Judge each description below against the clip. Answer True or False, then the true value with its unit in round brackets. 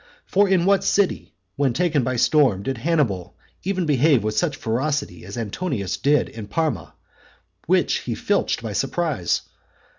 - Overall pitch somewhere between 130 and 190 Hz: True (135 Hz)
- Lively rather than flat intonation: True (6.9 semitones)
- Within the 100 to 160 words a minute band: True (150 wpm)